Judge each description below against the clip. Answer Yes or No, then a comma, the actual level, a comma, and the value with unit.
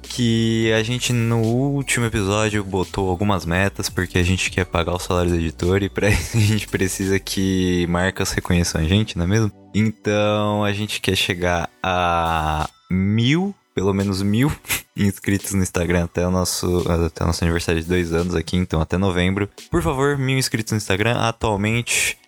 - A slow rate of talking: No, average, 180 wpm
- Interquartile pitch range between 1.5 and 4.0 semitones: Yes, average, 3.6 semitones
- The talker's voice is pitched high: No, low, 100 Hz